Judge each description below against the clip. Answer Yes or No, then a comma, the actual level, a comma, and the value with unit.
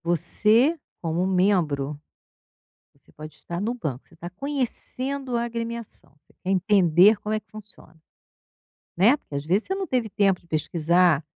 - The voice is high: Yes, high, 195 Hz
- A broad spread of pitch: Yes, wide, 5.8 semitones